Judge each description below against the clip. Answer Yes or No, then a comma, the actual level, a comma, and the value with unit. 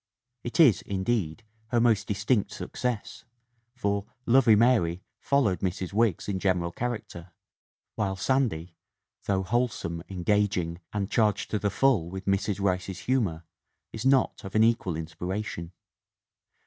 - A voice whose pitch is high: No, low, 100 Hz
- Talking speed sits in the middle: No, slow, 130 wpm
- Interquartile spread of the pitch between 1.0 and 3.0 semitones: No, average, 4.1 semitones